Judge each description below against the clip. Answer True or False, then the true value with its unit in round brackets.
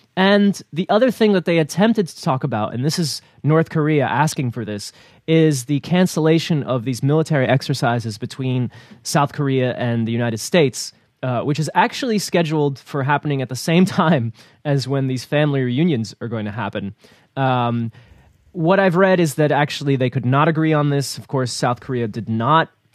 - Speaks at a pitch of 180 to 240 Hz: False (140 Hz)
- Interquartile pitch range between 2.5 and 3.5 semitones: False (4.7 semitones)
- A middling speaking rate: True (185 wpm)